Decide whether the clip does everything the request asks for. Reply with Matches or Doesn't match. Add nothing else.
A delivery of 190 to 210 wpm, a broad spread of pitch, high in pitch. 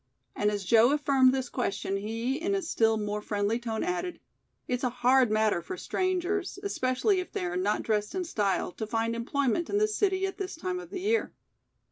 Matches